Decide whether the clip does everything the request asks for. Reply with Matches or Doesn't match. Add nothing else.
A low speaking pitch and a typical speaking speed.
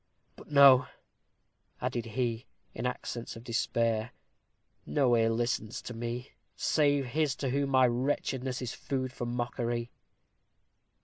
Doesn't match